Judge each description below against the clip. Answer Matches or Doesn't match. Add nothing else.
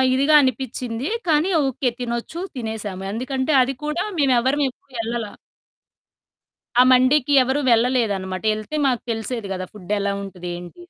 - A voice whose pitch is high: Matches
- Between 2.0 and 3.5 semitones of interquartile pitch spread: Doesn't match